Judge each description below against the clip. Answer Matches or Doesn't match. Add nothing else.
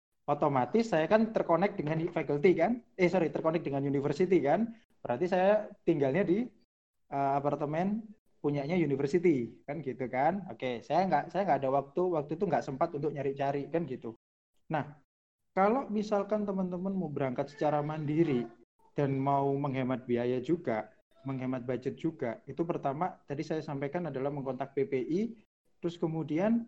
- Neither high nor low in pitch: Matches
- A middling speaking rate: Doesn't match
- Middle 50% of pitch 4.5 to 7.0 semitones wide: Matches